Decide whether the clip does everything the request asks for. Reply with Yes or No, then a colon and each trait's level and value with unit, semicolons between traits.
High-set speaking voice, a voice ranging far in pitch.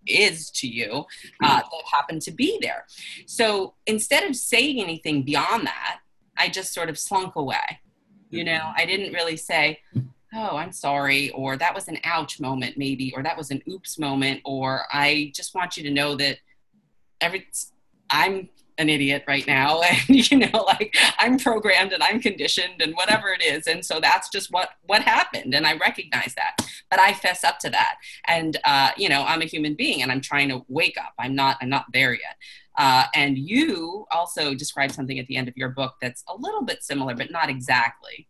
No: medium, 160 Hz; wide, 6.6 semitones